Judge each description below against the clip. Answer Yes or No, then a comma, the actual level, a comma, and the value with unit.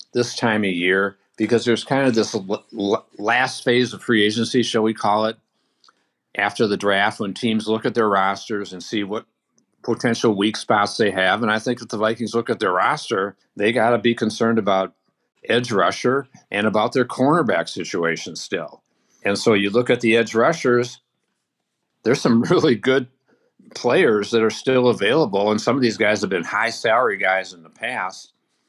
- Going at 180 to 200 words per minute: Yes, average, 185 wpm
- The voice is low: Yes, low, 110 Hz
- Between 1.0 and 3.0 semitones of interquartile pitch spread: Yes, narrow, 2.6 semitones